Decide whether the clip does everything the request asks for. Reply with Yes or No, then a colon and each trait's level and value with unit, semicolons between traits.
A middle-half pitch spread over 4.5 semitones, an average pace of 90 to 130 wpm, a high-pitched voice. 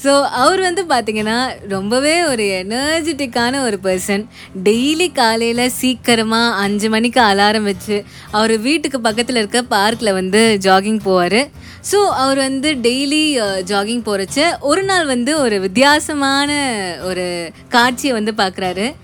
Yes: average, 5.2 semitones; average, 125 wpm; high, 235 Hz